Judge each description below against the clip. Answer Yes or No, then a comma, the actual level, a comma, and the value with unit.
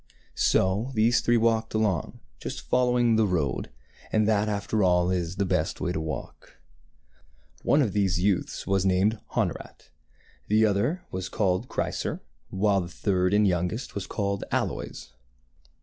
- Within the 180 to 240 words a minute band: No, average, 150 wpm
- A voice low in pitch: Yes, low, 100 Hz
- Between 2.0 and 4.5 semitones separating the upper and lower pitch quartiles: Yes, average, 3.1 semitones